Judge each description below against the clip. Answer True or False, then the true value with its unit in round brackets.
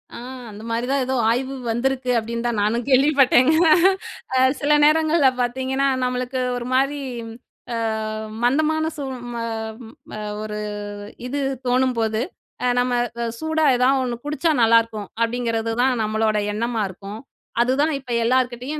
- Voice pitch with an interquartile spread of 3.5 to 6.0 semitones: False (3.0 semitones)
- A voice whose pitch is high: True (250 Hz)